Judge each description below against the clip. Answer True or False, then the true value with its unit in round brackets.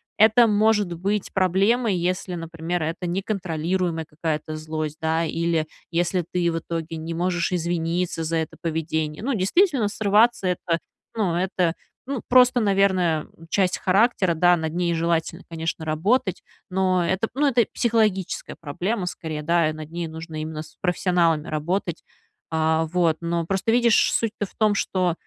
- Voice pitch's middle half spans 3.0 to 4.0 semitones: True (3.3 semitones)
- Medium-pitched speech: True (175 Hz)